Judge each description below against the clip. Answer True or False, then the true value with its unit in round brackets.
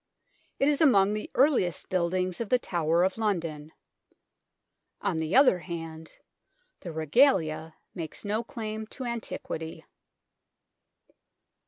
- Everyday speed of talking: False (115 wpm)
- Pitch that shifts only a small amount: False (5.6 semitones)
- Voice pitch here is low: False (185 Hz)